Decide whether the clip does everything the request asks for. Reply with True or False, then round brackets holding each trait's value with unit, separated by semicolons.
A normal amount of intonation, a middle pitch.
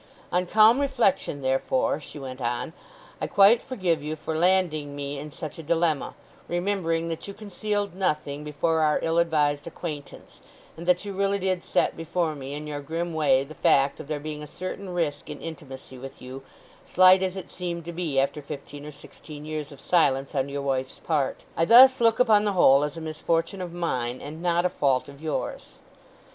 True (3.9 semitones; 160 Hz)